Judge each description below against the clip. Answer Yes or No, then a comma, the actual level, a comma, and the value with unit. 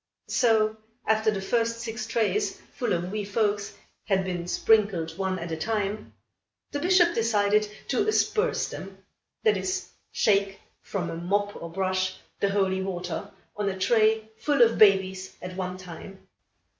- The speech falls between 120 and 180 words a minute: Yes, average, 155 wpm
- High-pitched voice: Yes, high, 205 Hz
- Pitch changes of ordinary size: Yes, average, 3.0 semitones